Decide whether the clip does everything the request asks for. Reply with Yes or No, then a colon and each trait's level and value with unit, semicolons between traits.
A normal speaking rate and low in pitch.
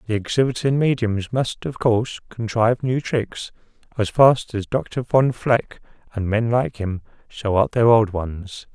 Yes: average, 165 wpm; low, 115 Hz